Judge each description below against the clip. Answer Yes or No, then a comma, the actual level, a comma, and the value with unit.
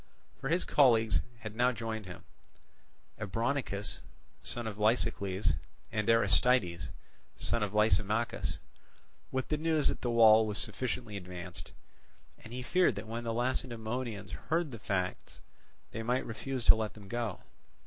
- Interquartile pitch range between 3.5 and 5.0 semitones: No, average, 2.9 semitones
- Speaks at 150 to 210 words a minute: No, average, 140 wpm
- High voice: No, low, 110 Hz